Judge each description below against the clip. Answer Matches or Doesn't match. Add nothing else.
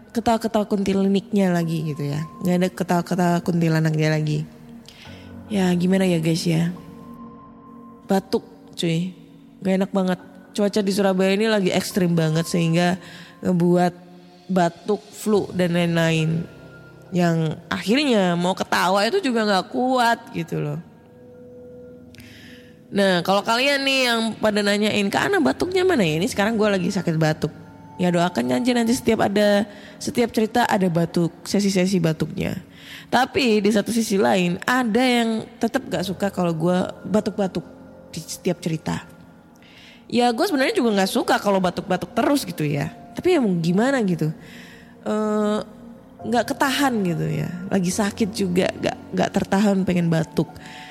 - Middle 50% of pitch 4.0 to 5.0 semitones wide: Matches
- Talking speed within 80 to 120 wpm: Doesn't match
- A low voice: Doesn't match